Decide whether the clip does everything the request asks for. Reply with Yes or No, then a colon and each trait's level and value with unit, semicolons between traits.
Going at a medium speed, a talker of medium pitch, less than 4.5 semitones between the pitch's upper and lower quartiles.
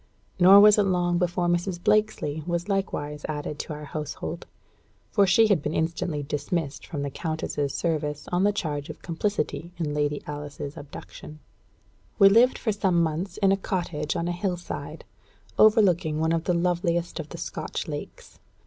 Yes: average, 170 wpm; medium, 170 Hz; average, 4.0 semitones